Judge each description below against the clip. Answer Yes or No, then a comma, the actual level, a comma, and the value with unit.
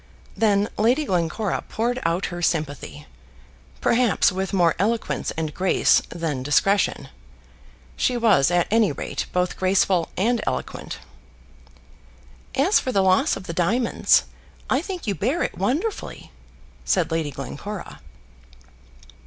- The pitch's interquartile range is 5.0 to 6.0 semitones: Yes, wide, 5.5 semitones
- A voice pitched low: No, high, 195 Hz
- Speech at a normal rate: No, slow, 125 wpm